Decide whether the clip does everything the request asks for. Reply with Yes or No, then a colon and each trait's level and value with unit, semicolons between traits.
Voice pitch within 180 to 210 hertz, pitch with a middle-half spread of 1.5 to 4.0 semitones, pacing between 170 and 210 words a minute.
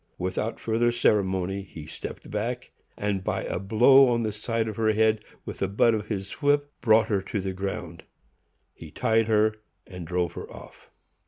No: low, 105 Hz; average, 2.8 semitones; average, 180 wpm